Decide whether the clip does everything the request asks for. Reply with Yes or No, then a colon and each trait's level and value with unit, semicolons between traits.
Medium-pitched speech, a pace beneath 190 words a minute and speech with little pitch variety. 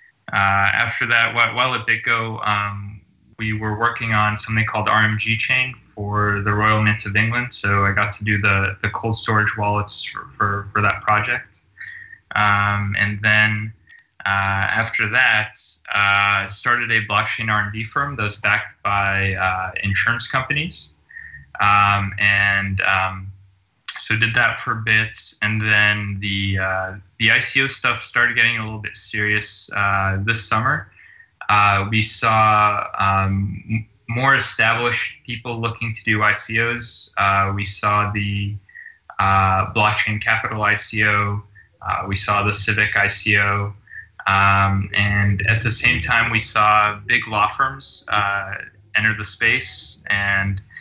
No: low, 105 Hz; average, 145 wpm; narrow, 1.8 semitones